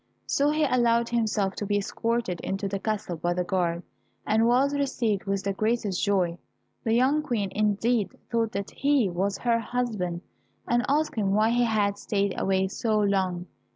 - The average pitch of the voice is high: Yes, high, 210 Hz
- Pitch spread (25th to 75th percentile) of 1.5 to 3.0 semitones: No, average, 3.5 semitones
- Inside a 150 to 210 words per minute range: Yes, average, 175 wpm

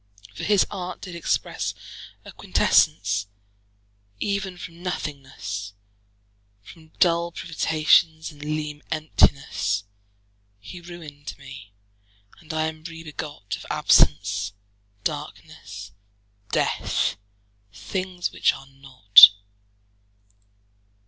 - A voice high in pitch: No, medium, 155 Hz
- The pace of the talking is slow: Yes, slow, 90 wpm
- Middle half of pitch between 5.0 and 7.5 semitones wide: No, average, 4.3 semitones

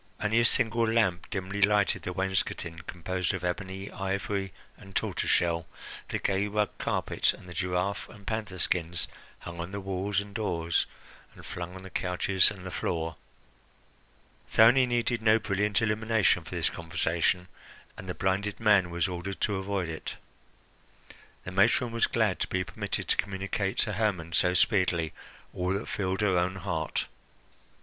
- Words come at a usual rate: Yes, average, 160 wpm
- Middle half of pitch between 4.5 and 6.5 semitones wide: No, narrow, 2.6 semitones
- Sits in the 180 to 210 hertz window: No, very low, 95 Hz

